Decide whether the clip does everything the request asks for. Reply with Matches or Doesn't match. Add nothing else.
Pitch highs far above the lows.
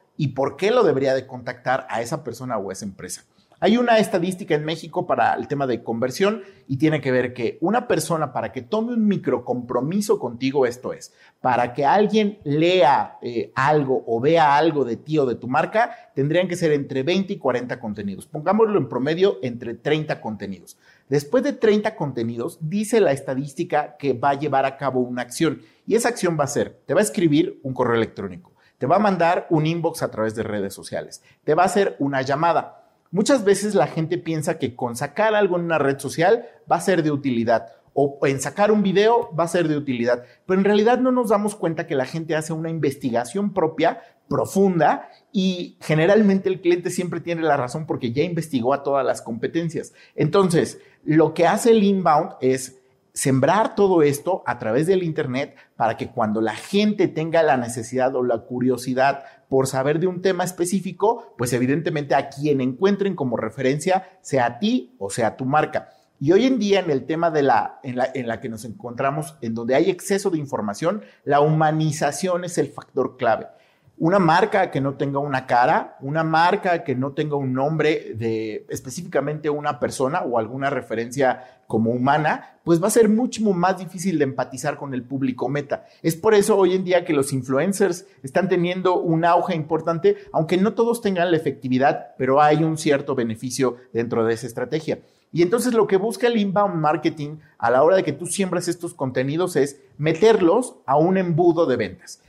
Matches